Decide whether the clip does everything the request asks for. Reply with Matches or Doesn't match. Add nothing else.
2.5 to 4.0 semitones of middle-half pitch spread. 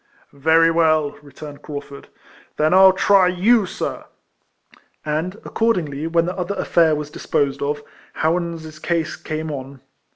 Matches